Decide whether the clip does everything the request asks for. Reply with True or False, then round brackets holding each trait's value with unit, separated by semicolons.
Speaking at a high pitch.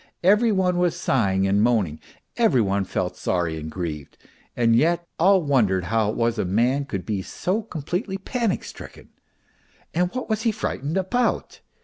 False (135 Hz)